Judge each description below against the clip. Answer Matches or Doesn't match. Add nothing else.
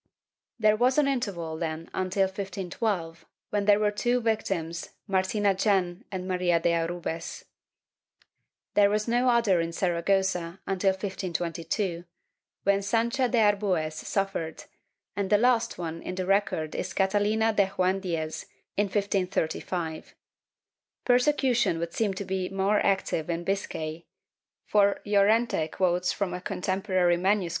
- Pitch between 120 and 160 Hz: Doesn't match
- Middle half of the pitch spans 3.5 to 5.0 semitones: Doesn't match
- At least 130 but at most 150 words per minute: Matches